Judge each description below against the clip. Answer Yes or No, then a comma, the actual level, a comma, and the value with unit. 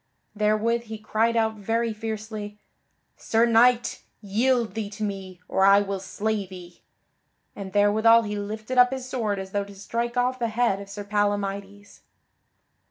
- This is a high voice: Yes, high, 215 Hz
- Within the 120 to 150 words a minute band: No, average, 160 wpm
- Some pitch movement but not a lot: No, narrow, 2.3 semitones